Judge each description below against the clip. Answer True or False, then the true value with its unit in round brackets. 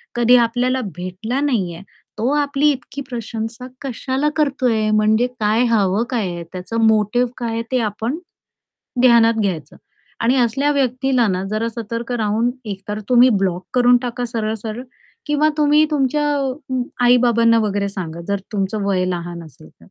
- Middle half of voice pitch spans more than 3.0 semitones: True (3.6 semitones)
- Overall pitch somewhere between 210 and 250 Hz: True (230 Hz)